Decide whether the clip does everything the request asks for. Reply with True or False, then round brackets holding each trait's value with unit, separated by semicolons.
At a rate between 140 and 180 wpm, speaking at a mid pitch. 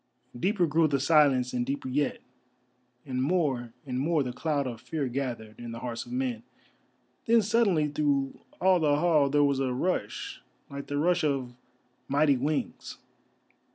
True (160 wpm; 145 Hz)